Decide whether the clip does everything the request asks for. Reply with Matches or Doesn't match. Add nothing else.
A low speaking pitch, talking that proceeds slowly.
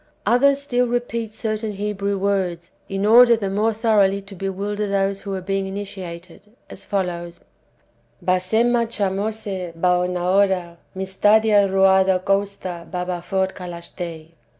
Doesn't match